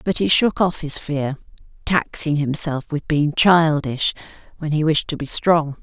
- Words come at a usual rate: Yes, average, 175 wpm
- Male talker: No, female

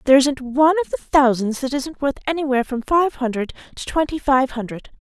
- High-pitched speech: Yes, very high, 270 Hz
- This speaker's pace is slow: No, average, 200 wpm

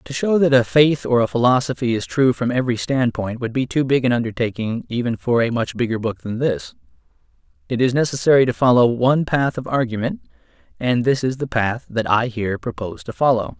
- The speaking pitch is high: No, low, 125 Hz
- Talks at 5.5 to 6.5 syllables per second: Yes, 5.8 syllables/s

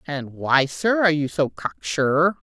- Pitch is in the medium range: Yes, medium, 155 Hz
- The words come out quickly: No, average, 190 wpm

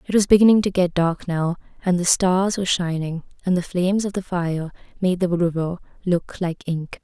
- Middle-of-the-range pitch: Yes, medium, 180 Hz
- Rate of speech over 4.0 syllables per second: Yes, 5.1 syllables/s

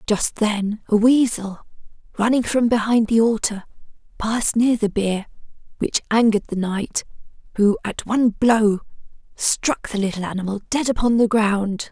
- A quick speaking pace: No, average, 145 wpm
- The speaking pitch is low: No, high, 220 Hz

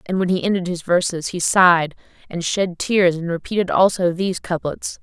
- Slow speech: No, average, 190 wpm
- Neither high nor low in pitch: Yes, medium, 180 Hz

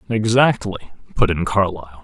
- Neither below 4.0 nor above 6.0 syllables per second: Yes, 4.9 syllables/s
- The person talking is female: No, male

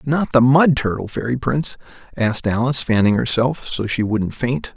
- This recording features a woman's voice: No, male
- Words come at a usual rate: Yes, average, 175 wpm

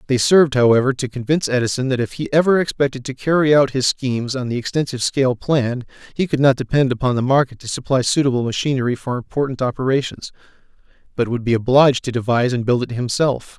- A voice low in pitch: Yes, low, 130 Hz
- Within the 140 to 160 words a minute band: No, average, 200 wpm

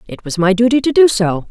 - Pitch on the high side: Yes, high, 220 Hz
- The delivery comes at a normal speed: No, fast, 280 wpm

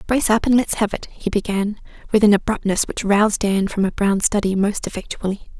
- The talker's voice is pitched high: Yes, high, 205 Hz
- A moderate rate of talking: No, fast, 215 wpm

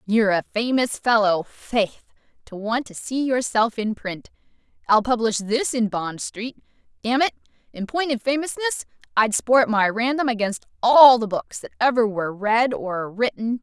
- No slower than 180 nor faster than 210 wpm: No, average, 170 wpm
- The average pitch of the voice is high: Yes, high, 230 Hz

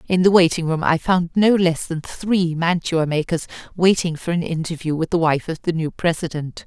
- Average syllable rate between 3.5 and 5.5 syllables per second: Yes, 5.0 syllables/s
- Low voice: No, medium, 170 Hz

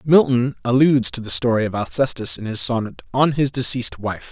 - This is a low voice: Yes, low, 125 Hz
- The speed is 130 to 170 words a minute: No, average, 195 wpm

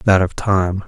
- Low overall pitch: Yes, very low, 95 Hz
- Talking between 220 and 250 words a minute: No, fast, 205 wpm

